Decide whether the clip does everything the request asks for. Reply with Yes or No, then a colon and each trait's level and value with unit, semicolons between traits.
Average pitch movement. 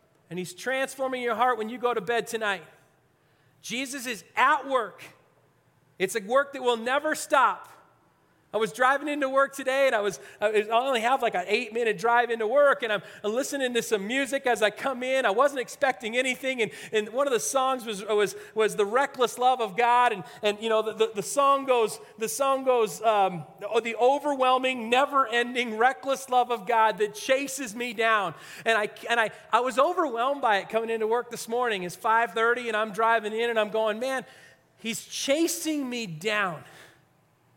Yes: average, 3.6 semitones